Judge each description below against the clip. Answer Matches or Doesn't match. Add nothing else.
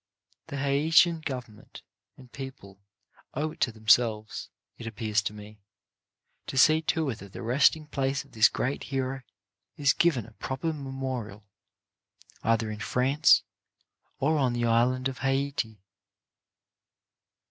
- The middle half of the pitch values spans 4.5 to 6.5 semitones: Doesn't match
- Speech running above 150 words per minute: Doesn't match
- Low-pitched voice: Matches